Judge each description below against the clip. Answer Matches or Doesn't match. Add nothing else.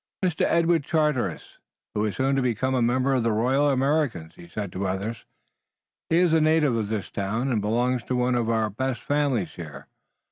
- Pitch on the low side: Matches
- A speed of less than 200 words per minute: Doesn't match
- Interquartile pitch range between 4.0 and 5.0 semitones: Matches